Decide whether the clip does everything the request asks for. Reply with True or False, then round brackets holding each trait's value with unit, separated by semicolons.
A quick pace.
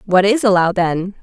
False (195 wpm)